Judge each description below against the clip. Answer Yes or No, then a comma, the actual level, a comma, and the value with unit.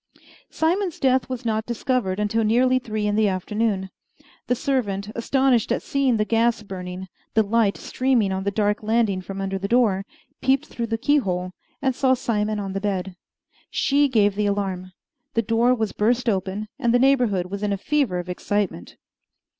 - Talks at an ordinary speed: Yes, average, 180 wpm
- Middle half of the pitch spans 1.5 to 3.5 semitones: No, average, 4.1 semitones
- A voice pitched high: Yes, high, 215 Hz